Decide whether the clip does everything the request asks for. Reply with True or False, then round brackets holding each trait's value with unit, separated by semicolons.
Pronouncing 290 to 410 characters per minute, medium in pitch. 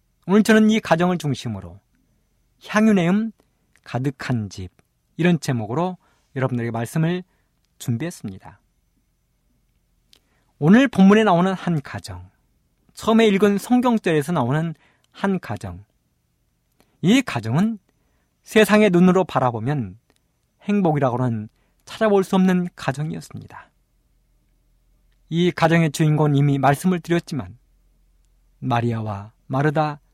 False (250 characters per minute; 145 Hz)